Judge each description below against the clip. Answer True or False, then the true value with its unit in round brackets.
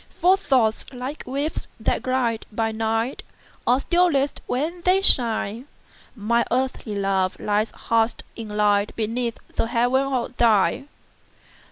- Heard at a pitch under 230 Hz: False (235 Hz)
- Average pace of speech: False (115 wpm)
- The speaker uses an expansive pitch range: False (3.4 semitones)